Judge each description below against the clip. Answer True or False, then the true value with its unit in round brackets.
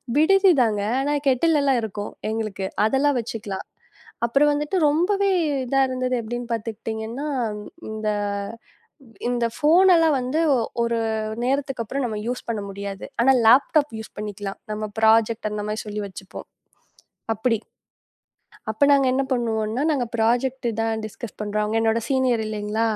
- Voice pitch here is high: True (235 Hz)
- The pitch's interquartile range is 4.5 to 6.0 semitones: False (3.9 semitones)